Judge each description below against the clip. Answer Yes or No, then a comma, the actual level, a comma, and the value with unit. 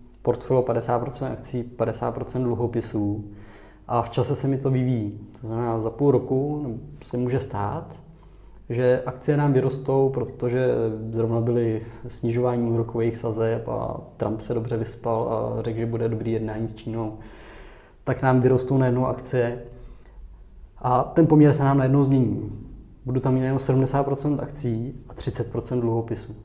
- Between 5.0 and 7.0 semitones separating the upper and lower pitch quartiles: No, narrow, 2.4 semitones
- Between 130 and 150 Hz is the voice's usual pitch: No, low, 120 Hz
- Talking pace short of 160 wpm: Yes, average, 145 wpm